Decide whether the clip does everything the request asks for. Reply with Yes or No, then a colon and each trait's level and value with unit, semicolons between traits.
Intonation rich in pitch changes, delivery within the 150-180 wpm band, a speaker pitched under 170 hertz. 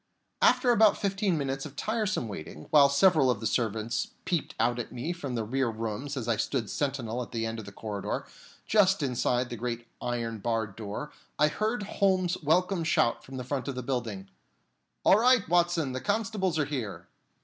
No: wide, 7.3 semitones; average, 190 wpm; low, 135 Hz